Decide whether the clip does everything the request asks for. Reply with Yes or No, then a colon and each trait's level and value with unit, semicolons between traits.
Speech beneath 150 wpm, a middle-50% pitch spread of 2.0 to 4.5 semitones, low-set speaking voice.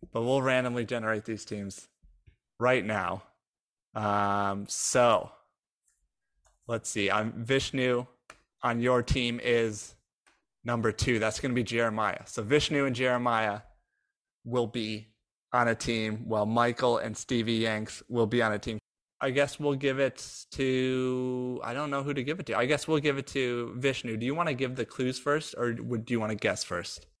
No: average, 180 wpm; average, 2.8 semitones; low, 120 Hz